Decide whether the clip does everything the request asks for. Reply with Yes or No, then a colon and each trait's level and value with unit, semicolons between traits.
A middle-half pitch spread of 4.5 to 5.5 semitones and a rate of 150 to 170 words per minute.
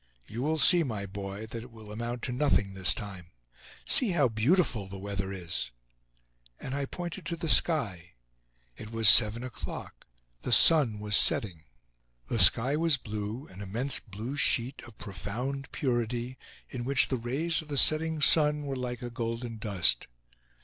Yes: average, 5.1 semitones; average, 165 wpm